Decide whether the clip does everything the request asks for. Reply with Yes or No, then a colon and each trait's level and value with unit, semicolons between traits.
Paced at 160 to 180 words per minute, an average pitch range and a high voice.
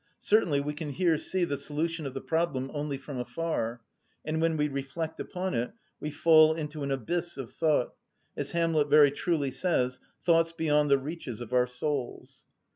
No: average, 175 wpm; average, 3.3 semitones; medium, 150 Hz